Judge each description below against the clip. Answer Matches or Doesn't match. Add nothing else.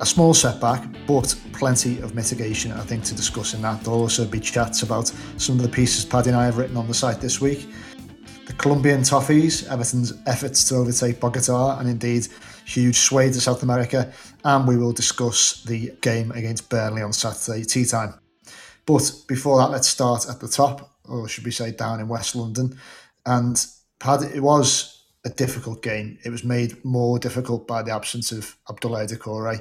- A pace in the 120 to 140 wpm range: Doesn't match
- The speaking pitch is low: Matches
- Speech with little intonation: Matches